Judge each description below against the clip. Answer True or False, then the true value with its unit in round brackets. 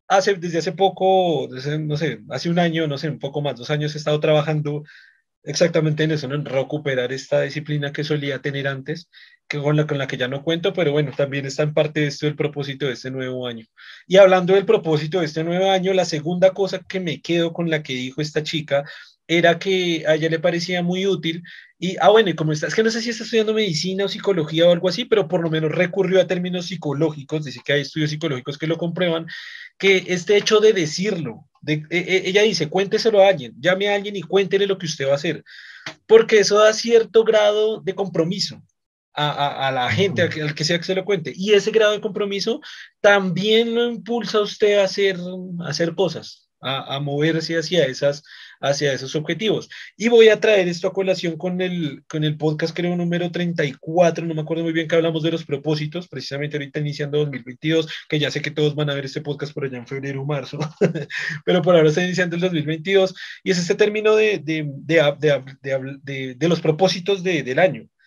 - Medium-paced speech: False (225 wpm)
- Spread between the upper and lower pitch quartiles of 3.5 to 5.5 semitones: True (4.3 semitones)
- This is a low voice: False (165 Hz)